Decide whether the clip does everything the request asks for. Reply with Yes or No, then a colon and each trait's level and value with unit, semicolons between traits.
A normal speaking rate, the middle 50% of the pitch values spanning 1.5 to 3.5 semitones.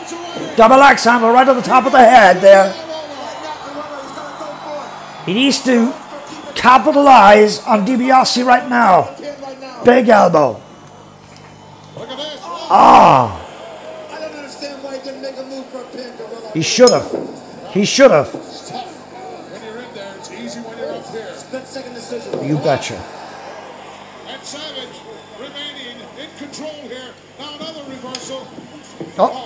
No: slow, 130 wpm; narrow, 2.4 semitones